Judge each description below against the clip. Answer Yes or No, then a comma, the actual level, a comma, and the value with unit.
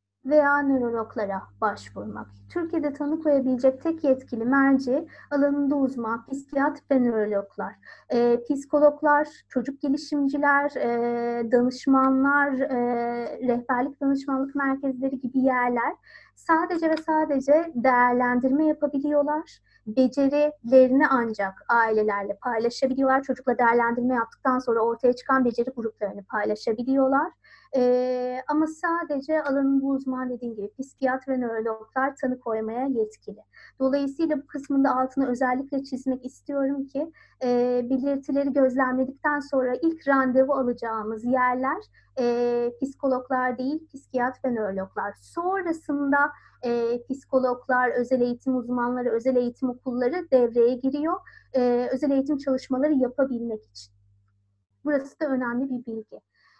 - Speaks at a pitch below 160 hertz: No, very high, 260 Hz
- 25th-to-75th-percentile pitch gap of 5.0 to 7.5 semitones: No, average, 2.7 semitones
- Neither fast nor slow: Yes, average, 110 wpm